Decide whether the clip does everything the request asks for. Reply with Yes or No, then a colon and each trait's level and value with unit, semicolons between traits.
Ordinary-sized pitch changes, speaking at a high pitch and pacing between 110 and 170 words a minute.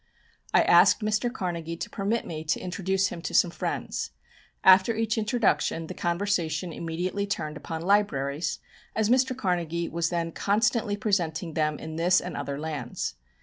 No: average, 3.8 semitones; medium, 180 Hz; average, 155 wpm